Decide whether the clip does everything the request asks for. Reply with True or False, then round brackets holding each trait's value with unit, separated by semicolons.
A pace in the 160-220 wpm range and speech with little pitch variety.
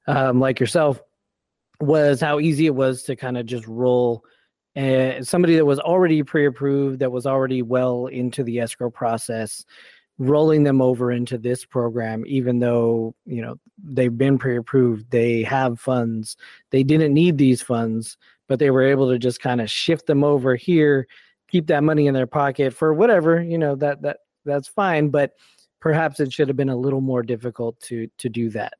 False (185 wpm; 3.1 semitones)